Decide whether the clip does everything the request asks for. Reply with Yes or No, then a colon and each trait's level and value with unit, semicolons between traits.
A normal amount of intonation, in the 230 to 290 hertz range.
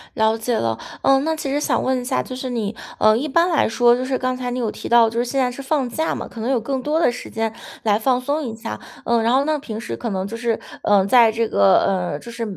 Yes: average, 3.0 semitones; high, 240 Hz